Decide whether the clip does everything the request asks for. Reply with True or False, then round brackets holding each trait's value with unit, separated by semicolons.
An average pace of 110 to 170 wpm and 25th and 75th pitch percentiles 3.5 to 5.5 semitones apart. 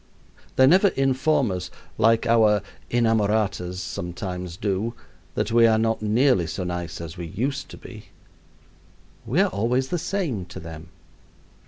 True (145 wpm; 5.1 semitones)